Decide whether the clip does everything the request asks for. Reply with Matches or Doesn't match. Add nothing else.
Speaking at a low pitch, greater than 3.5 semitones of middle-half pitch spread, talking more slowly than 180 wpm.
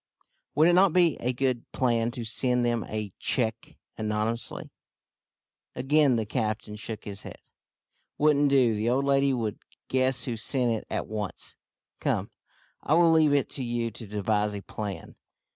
Matches